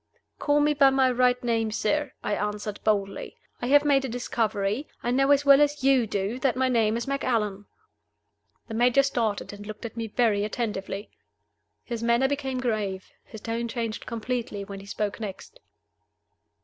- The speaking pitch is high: Yes, high, 235 Hz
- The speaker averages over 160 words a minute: Yes, average, 175 wpm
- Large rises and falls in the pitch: No, average, 4.0 semitones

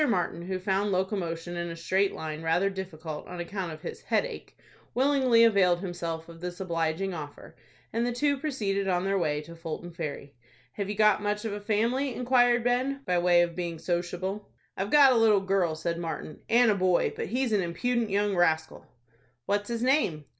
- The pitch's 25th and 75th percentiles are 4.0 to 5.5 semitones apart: Yes, average, 4.7 semitones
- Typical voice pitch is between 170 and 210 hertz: Yes, high, 190 Hz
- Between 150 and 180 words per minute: No, average, 190 wpm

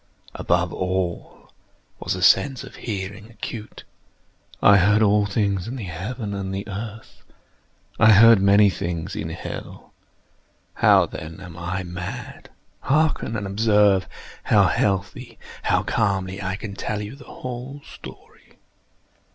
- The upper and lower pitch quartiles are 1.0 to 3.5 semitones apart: Yes, average, 2.7 semitones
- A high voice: No, low, 100 Hz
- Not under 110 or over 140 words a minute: Yes, slow, 135 wpm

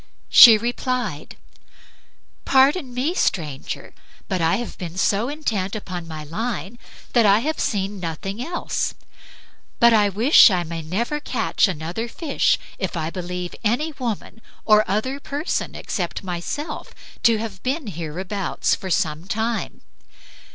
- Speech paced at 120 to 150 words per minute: Yes, slow, 135 wpm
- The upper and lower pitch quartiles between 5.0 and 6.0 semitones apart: Yes, wide, 5.4 semitones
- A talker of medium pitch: No, high, 210 Hz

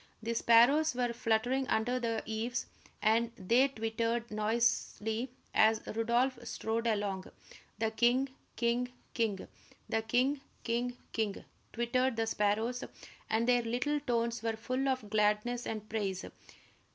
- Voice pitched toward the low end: No, high, 230 Hz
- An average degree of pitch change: No, narrow, 2.0 semitones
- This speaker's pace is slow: Yes, slow, 125 wpm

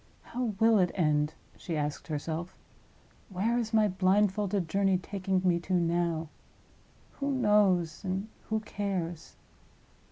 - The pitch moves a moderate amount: Yes, average, 3.5 semitones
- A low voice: No, medium, 185 Hz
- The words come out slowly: Yes, slow, 125 wpm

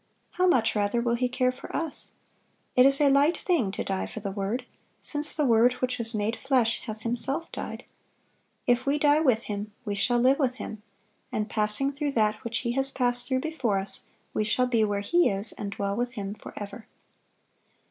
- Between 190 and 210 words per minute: Yes, average, 200 wpm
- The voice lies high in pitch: Yes, high, 245 Hz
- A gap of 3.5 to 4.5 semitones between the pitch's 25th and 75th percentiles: Yes, average, 4.1 semitones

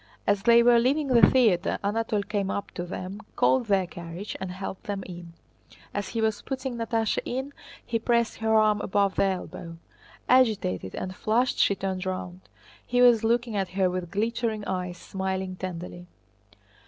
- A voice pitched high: Yes, high, 205 Hz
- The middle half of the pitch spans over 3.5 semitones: Yes, average, 3.9 semitones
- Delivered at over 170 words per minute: No, average, 165 wpm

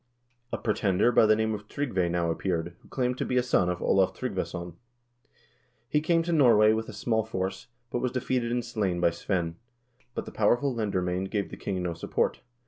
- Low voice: Yes, low, 105 Hz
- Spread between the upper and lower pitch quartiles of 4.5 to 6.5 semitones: Yes, average, 5.1 semitones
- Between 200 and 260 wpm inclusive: Yes, fast, 205 wpm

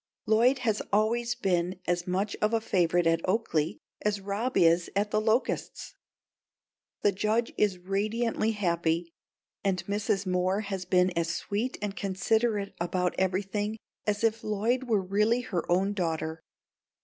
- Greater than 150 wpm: No, average, 145 wpm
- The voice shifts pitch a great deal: No, average, 3.2 semitones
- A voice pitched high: Yes, high, 200 Hz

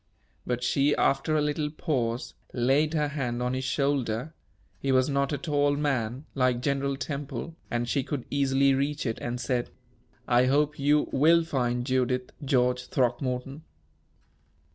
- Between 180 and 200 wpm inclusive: No, average, 150 wpm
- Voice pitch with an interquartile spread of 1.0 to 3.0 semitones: Yes, narrow, 2.6 semitones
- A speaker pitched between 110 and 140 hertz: Yes, low, 135 Hz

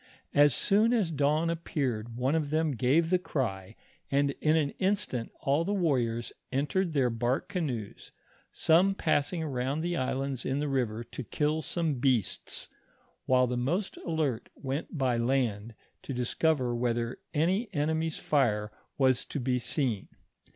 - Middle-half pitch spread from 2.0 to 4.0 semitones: No, average, 4.5 semitones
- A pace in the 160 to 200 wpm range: No, average, 150 wpm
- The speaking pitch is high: No, medium, 140 Hz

